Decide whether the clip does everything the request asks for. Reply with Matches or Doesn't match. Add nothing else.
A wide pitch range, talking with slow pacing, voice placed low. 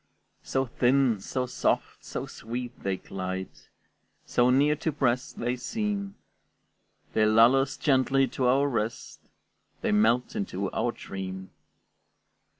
Doesn't match